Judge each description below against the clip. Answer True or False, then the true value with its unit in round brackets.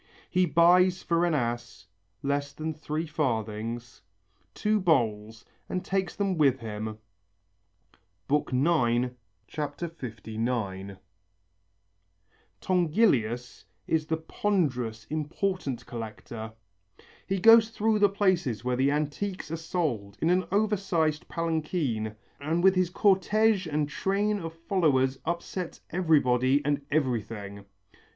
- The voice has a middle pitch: True (155 Hz)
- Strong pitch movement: True (7.1 semitones)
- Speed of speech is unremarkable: False (110 wpm)